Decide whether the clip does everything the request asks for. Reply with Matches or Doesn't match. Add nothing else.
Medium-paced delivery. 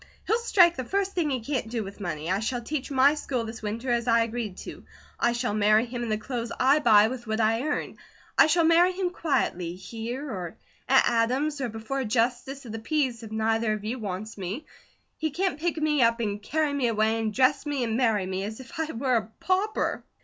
Doesn't match